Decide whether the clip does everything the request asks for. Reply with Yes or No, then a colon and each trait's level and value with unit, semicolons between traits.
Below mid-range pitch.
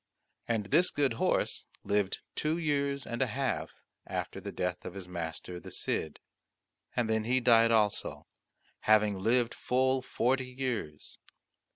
Yes: low, 115 Hz